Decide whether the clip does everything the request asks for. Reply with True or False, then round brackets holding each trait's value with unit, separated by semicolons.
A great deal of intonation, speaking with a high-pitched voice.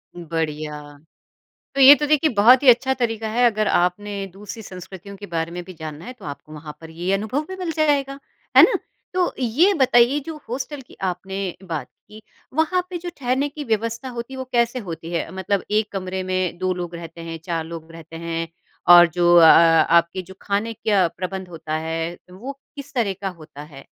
True (6.8 semitones; 195 Hz)